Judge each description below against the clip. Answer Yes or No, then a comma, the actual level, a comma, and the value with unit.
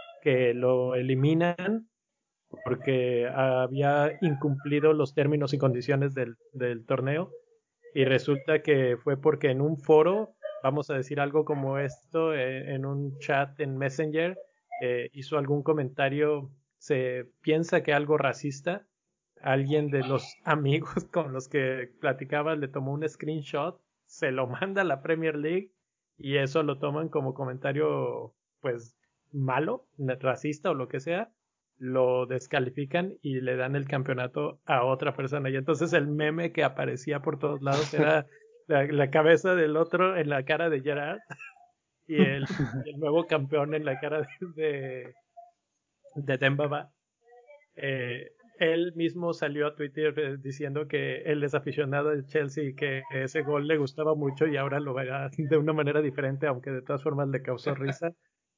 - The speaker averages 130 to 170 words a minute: Yes, average, 155 wpm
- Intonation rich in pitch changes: No, average, 2.7 semitones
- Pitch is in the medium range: Yes, medium, 145 Hz